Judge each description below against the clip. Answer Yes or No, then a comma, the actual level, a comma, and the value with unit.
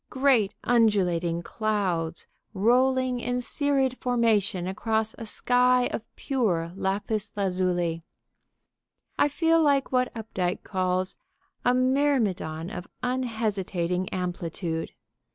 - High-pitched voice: Yes, high, 215 Hz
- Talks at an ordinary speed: No, slow, 100 wpm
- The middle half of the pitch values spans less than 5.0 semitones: No, wide, 5.6 semitones